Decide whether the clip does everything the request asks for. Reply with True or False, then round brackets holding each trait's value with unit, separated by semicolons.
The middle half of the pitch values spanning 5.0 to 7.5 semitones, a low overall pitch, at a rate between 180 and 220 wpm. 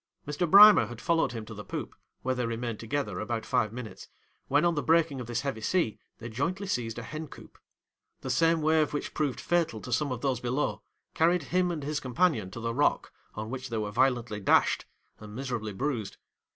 True (5.3 semitones; 130 Hz; 205 wpm)